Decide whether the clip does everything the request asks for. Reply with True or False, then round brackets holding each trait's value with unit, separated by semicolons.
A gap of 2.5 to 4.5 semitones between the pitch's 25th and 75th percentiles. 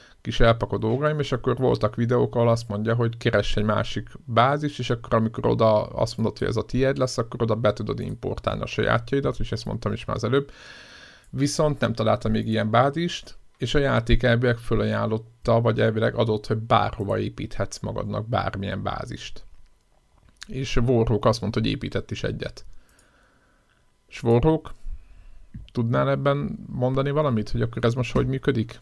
True (2.8 semitones)